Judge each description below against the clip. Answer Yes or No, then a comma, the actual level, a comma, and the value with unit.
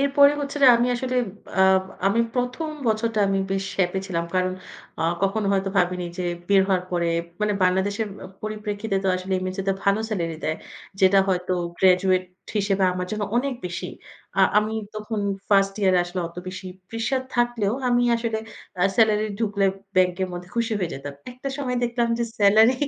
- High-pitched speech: Yes, high, 200 Hz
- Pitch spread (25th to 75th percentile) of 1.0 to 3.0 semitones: No, average, 3.7 semitones